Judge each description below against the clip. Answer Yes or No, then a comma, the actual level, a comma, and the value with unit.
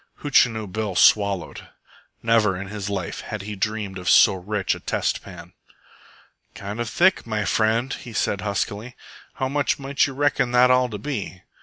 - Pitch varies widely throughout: No, average, 4.1 semitones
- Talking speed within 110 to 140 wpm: No, average, 170 wpm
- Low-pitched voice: Yes, low, 110 Hz